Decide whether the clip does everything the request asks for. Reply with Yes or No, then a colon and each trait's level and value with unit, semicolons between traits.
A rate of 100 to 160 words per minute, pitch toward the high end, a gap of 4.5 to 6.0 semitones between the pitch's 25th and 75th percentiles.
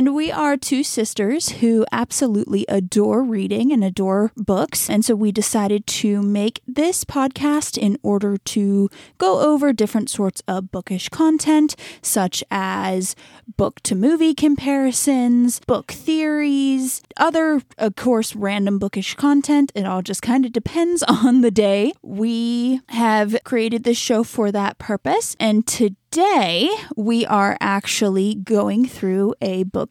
Yes: average, 140 wpm; high, 225 Hz; average, 5.1 semitones